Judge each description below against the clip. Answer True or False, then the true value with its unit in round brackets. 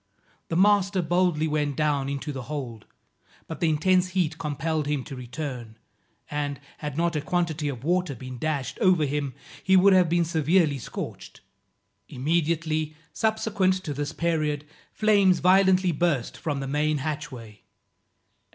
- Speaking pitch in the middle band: True (155 Hz)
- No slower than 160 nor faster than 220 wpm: False (145 wpm)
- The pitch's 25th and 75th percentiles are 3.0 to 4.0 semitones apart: True (3.7 semitones)